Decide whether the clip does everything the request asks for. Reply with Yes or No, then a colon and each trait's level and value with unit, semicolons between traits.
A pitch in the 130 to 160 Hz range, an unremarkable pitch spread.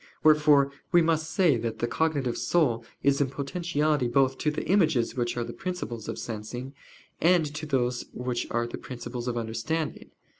Yes: low, 135 Hz; average, 4.6 semitones